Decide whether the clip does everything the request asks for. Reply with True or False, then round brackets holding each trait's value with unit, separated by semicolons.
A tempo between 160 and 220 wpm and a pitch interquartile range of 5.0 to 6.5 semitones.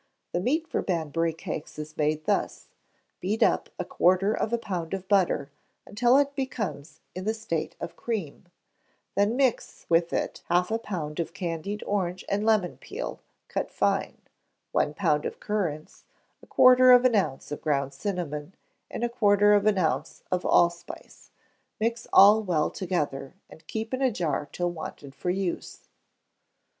True (165 wpm; 5.3 semitones)